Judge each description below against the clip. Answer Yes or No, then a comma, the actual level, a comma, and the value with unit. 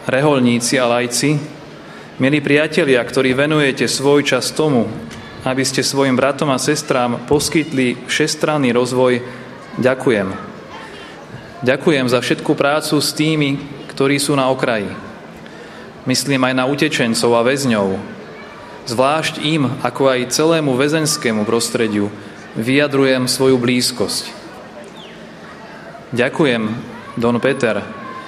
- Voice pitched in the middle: No, low, 130 Hz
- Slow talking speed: Yes, slow, 105 wpm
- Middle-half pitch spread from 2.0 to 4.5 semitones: Yes, average, 2.9 semitones